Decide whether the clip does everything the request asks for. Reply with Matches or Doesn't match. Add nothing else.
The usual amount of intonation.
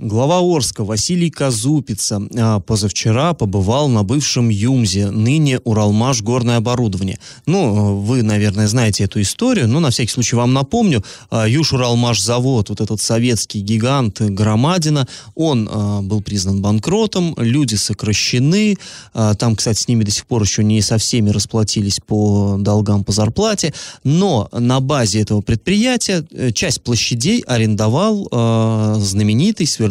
Matches